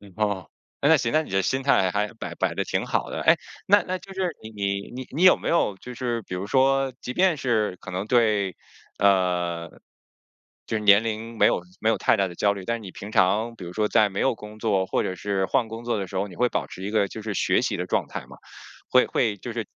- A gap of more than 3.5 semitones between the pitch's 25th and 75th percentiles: Yes, average, 4.0 semitones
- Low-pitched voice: Yes, low, 105 Hz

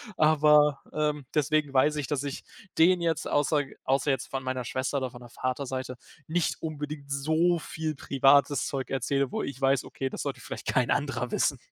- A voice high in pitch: No, medium, 140 Hz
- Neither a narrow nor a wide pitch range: No, narrow, 2.3 semitones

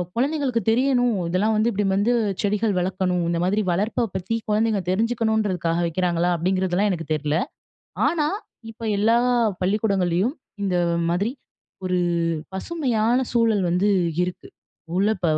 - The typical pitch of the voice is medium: No, high, 205 Hz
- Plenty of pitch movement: No, average, 3.9 semitones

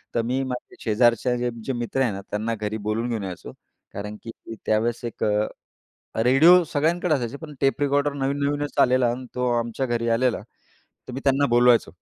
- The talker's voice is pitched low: Yes, low, 125 Hz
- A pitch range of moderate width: Yes, average, 3.2 semitones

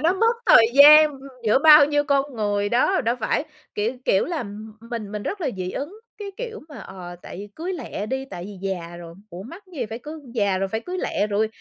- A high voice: Yes, high, 235 Hz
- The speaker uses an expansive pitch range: Yes, wide, 7.2 semitones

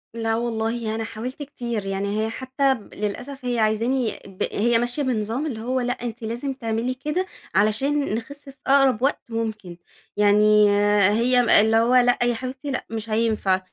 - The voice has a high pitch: Yes, high, 235 Hz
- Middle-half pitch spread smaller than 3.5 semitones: Yes, average, 2.9 semitones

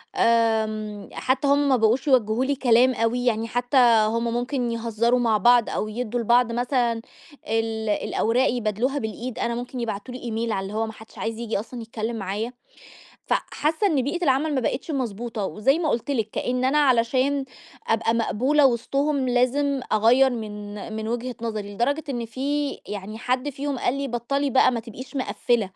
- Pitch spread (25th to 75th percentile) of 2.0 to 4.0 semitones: Yes, average, 2.9 semitones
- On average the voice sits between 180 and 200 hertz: No, high, 240 Hz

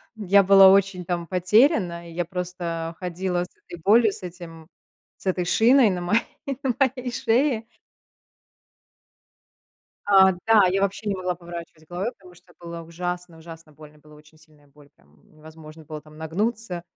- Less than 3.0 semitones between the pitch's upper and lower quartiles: No, average, 3.3 semitones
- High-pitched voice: No, medium, 180 Hz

